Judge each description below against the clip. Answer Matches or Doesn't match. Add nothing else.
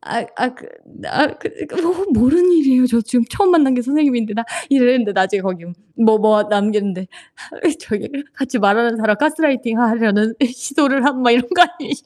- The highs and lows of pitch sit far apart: Doesn't match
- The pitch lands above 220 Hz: Matches